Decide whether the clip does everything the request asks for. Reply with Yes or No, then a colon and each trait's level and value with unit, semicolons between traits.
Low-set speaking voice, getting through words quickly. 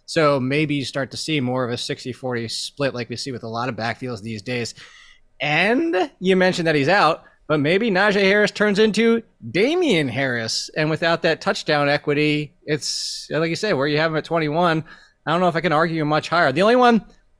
No: medium, 155 Hz; fast, 215 wpm